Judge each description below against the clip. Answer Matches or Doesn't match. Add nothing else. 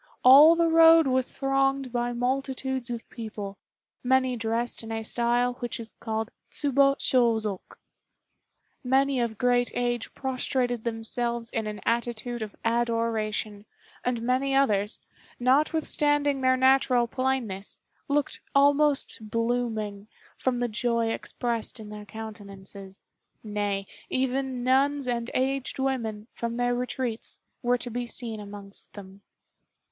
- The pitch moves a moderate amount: Matches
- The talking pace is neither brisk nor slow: Doesn't match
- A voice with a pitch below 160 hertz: Doesn't match